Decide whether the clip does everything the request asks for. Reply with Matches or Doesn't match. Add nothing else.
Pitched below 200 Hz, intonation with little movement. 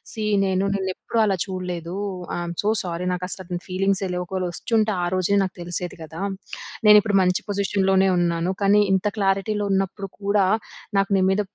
Matches